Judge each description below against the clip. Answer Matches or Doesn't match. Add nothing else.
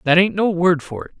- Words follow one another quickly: Matches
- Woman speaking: Doesn't match